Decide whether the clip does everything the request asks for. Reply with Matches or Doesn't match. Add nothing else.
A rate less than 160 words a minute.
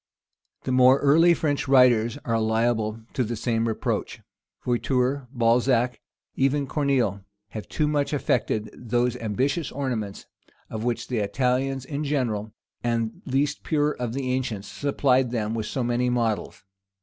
Matches